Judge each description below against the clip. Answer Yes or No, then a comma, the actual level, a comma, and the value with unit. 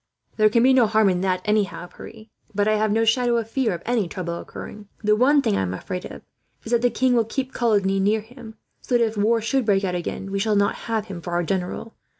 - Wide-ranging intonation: No, average, 3.2 semitones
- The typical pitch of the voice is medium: No, high, 215 Hz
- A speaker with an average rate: No, fast, 255 wpm